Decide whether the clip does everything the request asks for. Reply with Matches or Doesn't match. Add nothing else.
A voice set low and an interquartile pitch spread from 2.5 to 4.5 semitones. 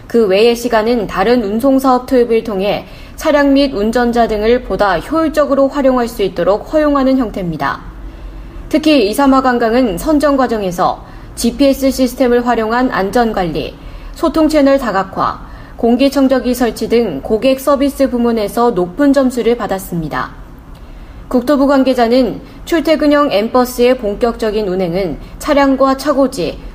Doesn't match